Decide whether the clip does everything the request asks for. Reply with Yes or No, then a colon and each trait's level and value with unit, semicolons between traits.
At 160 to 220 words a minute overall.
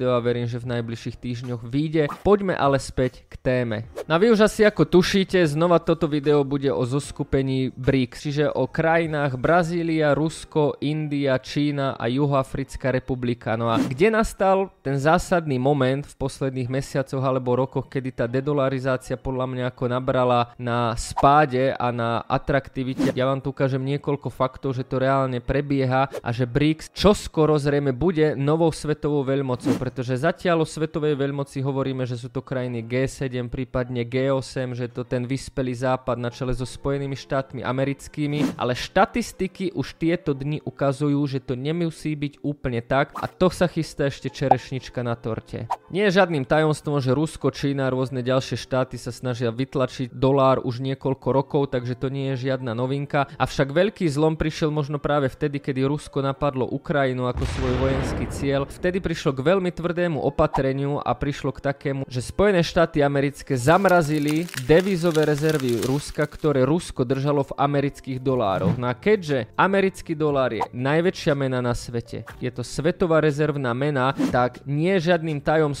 Yes: average, 165 wpm